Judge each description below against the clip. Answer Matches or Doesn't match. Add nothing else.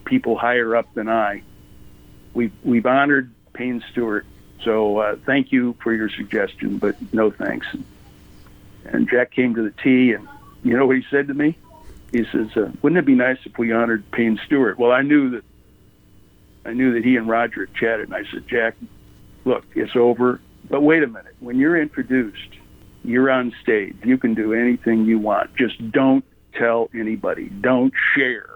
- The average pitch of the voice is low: Matches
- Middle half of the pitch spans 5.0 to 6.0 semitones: Doesn't match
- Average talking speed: Matches